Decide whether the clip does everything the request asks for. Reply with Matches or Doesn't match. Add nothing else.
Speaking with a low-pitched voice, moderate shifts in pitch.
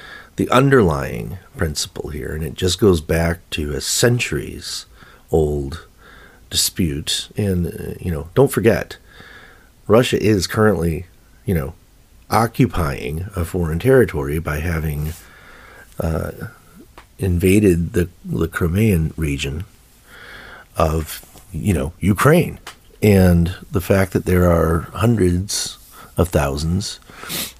Matches